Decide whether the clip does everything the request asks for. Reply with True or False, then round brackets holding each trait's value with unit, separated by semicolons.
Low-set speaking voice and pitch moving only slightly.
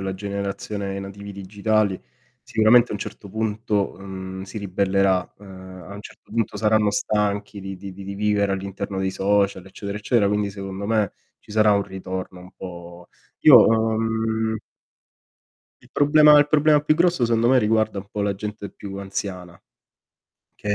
True (100 Hz; 2.1 semitones)